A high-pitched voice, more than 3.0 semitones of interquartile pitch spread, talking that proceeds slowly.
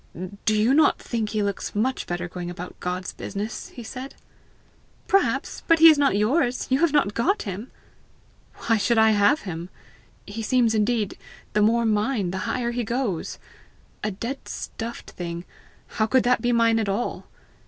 No: high, 225 Hz; average, 3.7 semitones; average, 175 wpm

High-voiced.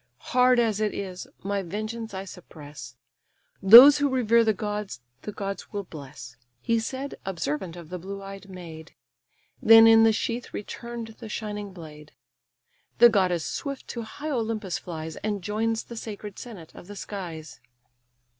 Yes: high, 205 Hz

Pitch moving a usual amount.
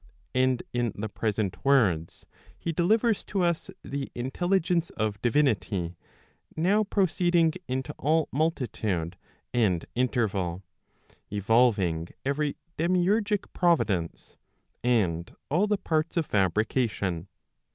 No: wide, 8.7 semitones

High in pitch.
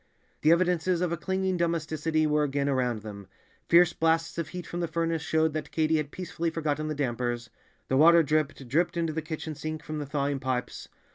No: medium, 155 Hz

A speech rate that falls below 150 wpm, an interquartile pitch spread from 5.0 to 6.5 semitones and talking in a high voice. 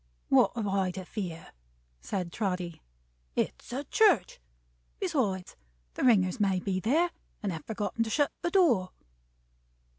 Yes: average, 140 wpm; wide, 5.4 semitones; high, 200 Hz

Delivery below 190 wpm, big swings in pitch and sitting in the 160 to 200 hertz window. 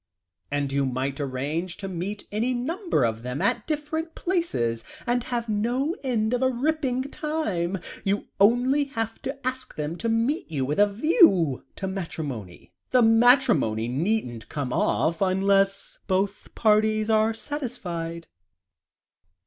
No: average, 140 wpm; wide, 8.0 semitones; high, 210 Hz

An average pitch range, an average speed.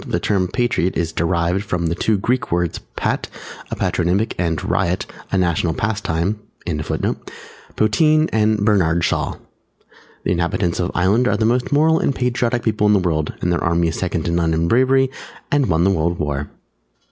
Yes: average, 4.8 semitones; average, 160 wpm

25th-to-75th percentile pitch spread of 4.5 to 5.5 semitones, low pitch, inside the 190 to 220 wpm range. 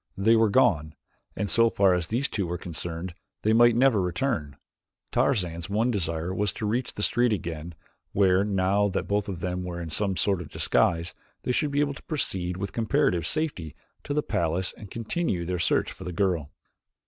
Yes: average, 4.8 semitones; very low, 95 Hz; average, 195 wpm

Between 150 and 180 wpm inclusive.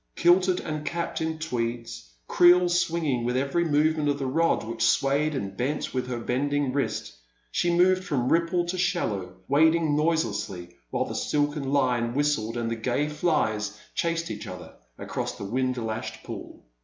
Yes: average, 170 wpm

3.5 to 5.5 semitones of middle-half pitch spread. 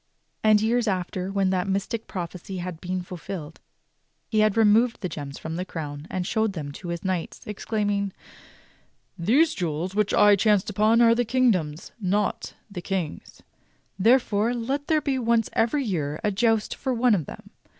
Yes: average, 4.1 semitones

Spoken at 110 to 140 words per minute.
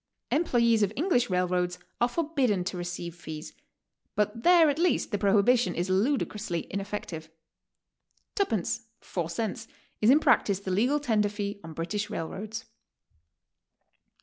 Yes: slow, 135 wpm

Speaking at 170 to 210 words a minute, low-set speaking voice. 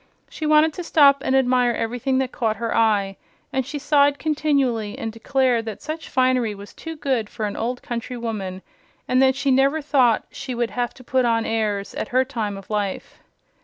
No: average, 200 wpm; very high, 250 Hz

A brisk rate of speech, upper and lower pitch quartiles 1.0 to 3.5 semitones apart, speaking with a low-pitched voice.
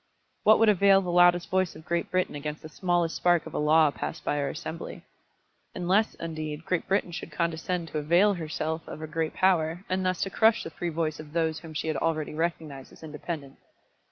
No: fast, 210 wpm; narrow, 2.4 semitones; medium, 165 Hz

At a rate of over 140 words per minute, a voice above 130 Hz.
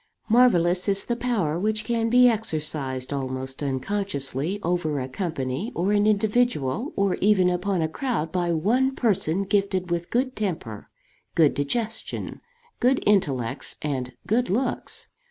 No: slow, 135 wpm; medium, 185 Hz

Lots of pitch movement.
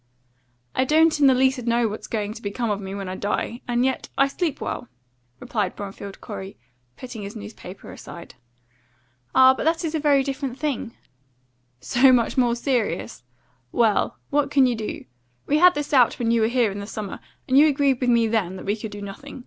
No: average, 4.6 semitones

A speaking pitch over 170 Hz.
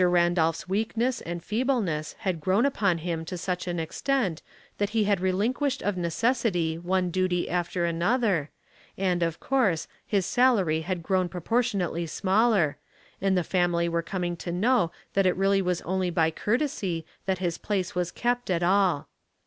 Yes: medium, 185 Hz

